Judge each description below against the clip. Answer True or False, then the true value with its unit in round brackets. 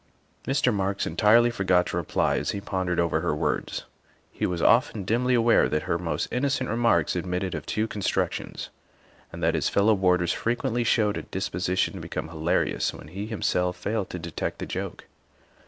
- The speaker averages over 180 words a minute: True (190 wpm)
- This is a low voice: True (95 Hz)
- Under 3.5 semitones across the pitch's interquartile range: False (4.4 semitones)